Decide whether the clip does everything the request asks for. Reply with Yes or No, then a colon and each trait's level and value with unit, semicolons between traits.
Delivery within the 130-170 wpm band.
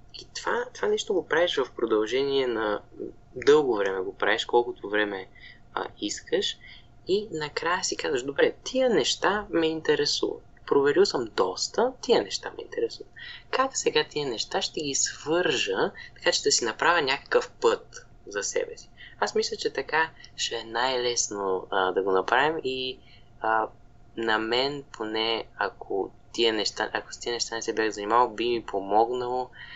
Yes: average, 160 wpm